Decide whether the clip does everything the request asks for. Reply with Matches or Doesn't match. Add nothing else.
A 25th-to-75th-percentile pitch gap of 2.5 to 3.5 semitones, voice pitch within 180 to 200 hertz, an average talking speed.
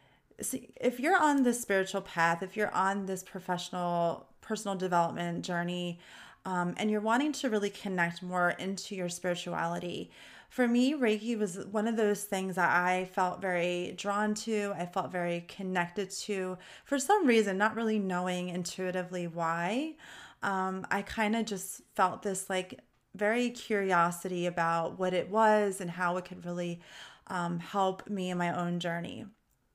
Matches